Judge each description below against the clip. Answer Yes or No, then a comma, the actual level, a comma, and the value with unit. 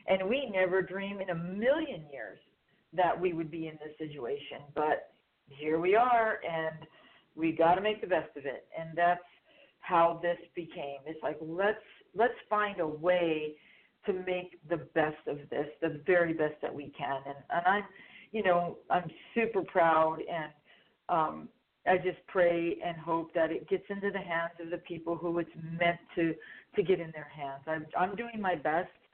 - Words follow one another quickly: No, average, 185 wpm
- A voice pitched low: No, medium, 170 Hz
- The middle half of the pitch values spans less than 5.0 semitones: Yes, average, 2.9 semitones